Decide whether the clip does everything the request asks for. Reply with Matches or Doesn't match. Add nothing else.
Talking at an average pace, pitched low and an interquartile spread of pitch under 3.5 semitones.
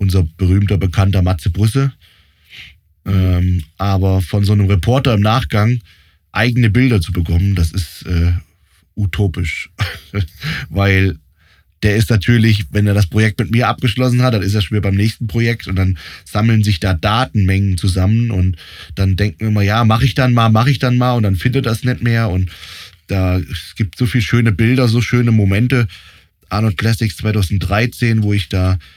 Doesn't match